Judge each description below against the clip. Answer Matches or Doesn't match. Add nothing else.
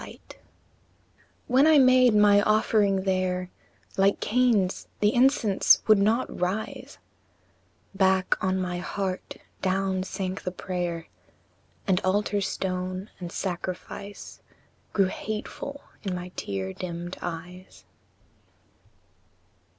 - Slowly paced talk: Matches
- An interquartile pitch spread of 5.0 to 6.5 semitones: Doesn't match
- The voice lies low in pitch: Doesn't match